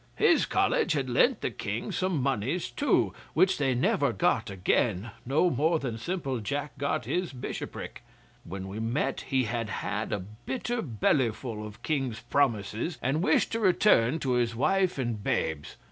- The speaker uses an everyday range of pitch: No, wide, 6.5 semitones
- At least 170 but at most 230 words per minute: No, average, 160 wpm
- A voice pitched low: Yes, low, 130 Hz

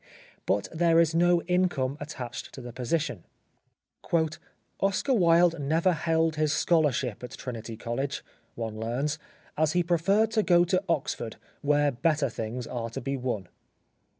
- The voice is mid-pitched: Yes, medium, 150 Hz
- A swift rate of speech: No, average, 150 wpm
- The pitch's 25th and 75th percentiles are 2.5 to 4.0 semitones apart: No, wide, 5.4 semitones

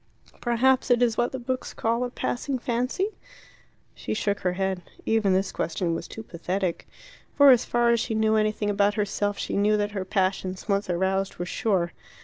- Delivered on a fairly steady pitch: No, average, 3.8 semitones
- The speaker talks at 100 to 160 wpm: No, average, 185 wpm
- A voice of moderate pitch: No, high, 210 Hz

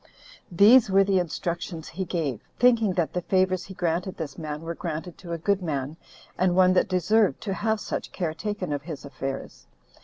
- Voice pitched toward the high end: No, medium, 180 Hz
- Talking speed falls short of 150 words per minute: No, average, 190 wpm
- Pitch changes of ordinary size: Yes, average, 3.2 semitones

